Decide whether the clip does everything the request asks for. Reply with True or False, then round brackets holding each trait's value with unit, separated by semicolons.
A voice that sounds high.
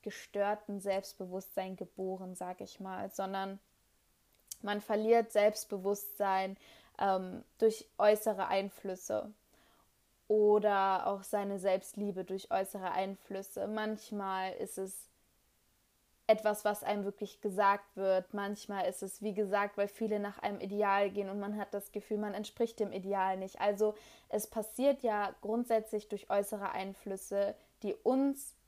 True (200 Hz)